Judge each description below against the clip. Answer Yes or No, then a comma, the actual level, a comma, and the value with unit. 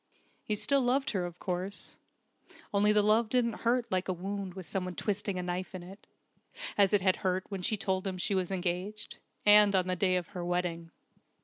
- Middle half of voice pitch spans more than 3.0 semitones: No, narrow, 2.4 semitones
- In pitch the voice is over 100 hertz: Yes, high, 190 Hz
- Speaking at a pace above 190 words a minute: Yes, fast, 205 wpm